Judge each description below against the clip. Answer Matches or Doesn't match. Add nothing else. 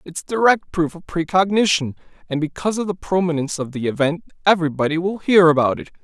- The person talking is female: Doesn't match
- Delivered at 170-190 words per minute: Matches